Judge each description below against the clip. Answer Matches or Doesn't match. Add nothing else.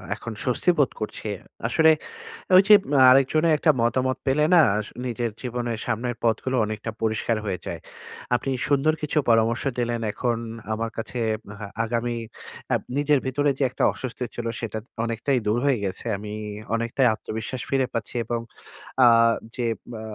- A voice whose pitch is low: Matches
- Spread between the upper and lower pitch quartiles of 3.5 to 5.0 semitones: Doesn't match